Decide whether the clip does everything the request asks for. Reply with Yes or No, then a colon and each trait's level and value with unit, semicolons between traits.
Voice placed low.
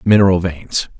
Yes: very low, 90 Hz